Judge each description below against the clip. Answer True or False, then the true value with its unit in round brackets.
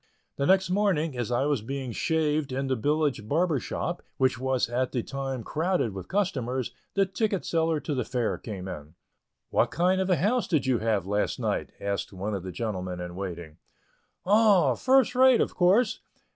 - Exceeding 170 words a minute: True (185 wpm)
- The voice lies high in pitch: False (135 Hz)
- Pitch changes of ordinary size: False (8.7 semitones)